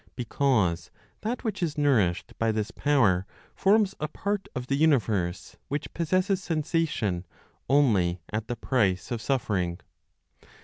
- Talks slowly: Yes, slow, 130 wpm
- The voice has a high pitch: No, low, 130 Hz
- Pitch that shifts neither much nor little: No, wide, 7.9 semitones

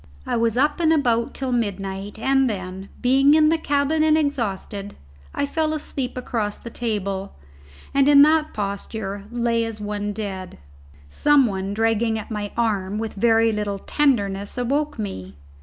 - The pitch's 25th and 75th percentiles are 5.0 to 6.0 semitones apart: Yes, average, 5.3 semitones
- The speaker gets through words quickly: No, average, 155 wpm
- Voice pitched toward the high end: Yes, high, 225 Hz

